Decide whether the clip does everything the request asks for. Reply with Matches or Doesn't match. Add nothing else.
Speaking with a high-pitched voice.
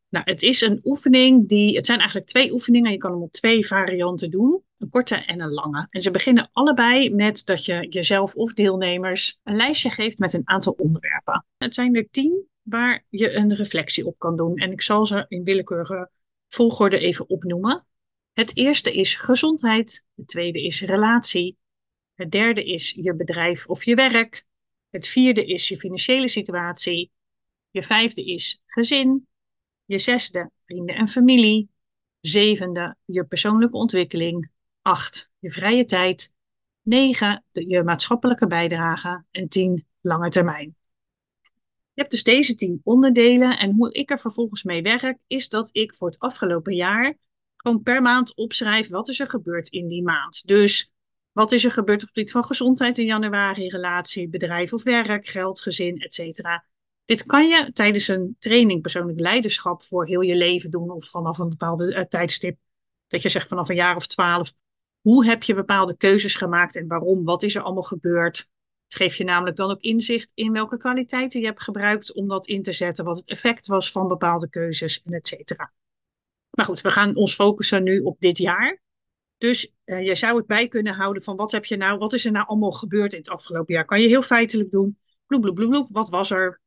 Matches